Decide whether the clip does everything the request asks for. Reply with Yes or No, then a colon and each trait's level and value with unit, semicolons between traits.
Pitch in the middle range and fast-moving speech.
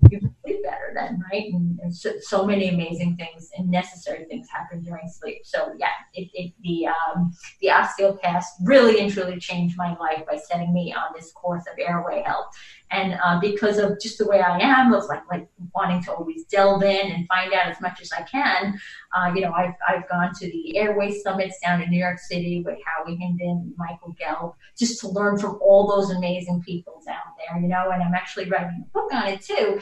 Yes: medium, 180 Hz; fast, 215 wpm